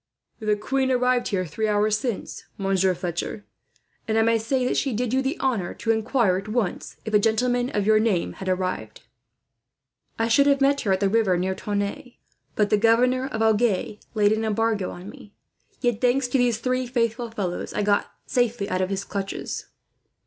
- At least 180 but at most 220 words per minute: Yes, average, 190 wpm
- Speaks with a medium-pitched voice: No, high, 220 Hz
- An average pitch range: Yes, average, 3.5 semitones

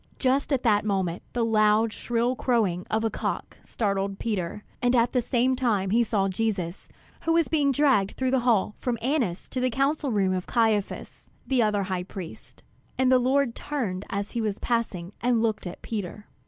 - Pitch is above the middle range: Yes, high, 225 Hz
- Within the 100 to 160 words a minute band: No, average, 190 wpm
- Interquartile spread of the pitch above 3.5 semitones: Yes, average, 4.2 semitones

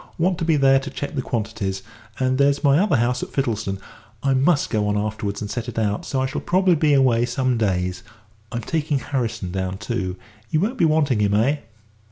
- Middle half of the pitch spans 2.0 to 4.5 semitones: No, average, 5.1 semitones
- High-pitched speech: No, low, 125 Hz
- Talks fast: Yes, fast, 215 wpm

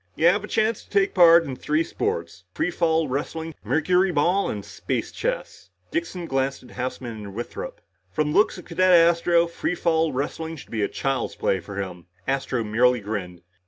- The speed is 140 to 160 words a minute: No, average, 180 wpm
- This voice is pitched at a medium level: Yes, medium, 160 Hz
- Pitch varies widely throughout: Yes, wide, 6.0 semitones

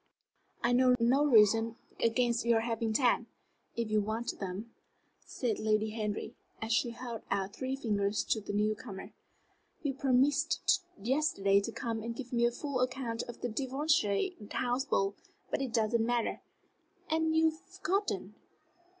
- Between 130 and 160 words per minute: Yes, average, 155 wpm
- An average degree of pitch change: Yes, average, 3.4 semitones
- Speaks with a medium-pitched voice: No, high, 235 Hz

